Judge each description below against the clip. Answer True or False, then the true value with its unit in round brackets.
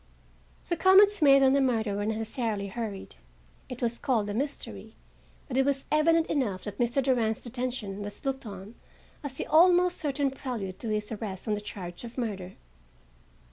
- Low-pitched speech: False (240 Hz)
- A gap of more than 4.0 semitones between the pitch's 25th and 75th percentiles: True (4.9 semitones)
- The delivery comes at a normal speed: True (175 wpm)